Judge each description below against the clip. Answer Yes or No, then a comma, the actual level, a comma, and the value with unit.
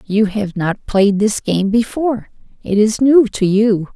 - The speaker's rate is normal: Yes, average, 165 wpm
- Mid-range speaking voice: No, high, 215 Hz